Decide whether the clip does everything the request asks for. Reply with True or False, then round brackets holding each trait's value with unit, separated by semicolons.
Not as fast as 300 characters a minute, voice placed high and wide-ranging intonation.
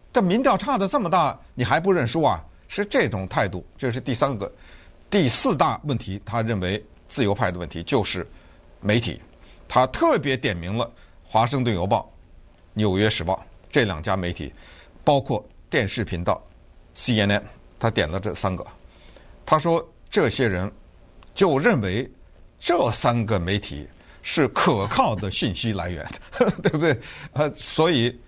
False (225 characters per minute; 105 Hz; 6.3 semitones)